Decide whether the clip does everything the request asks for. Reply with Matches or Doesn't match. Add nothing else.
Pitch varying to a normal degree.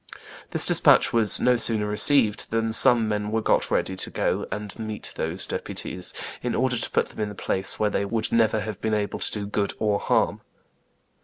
Doesn't match